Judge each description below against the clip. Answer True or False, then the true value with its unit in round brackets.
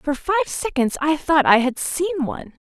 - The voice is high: True (305 Hz)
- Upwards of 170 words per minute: True (205 wpm)